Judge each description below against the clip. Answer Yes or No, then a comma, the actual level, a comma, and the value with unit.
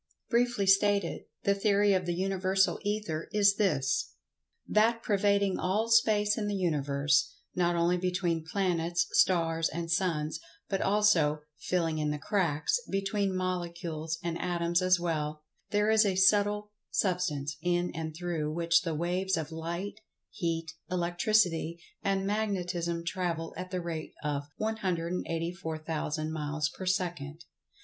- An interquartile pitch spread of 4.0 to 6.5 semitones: No, average, 3.3 semitones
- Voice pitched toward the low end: No, medium, 175 Hz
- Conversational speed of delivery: No, slow, 130 wpm